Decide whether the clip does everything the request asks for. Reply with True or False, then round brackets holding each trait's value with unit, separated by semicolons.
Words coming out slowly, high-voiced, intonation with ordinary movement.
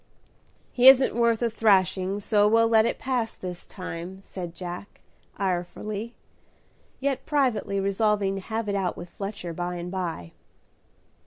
False (145 wpm; 200 Hz; 3.9 semitones)